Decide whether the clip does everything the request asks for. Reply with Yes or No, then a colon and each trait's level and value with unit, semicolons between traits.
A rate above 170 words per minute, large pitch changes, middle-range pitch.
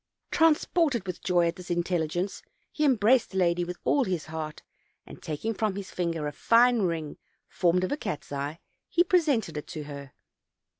Yes: average, 180 wpm; wide, 6.3 semitones; medium, 180 Hz